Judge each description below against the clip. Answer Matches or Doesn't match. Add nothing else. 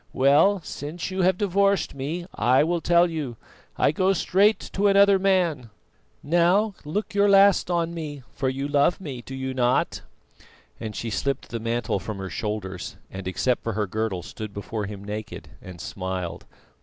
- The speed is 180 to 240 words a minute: Doesn't match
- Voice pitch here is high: Doesn't match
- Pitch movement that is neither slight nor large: Doesn't match